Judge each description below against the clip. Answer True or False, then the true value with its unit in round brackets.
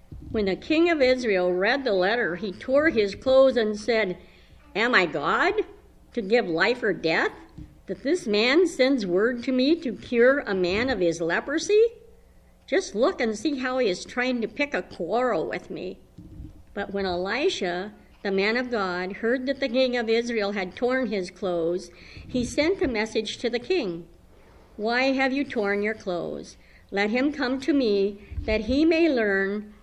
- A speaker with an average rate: True (180 wpm)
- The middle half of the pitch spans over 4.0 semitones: True (5.1 semitones)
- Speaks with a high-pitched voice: True (235 Hz)